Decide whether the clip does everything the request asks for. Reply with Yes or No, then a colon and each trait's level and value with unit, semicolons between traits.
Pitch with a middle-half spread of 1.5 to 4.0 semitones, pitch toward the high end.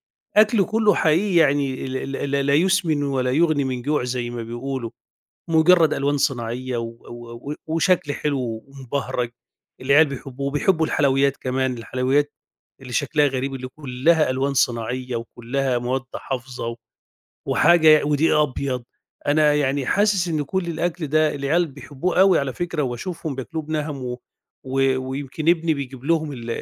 No: average, 3.5 semitones; medium, 140 Hz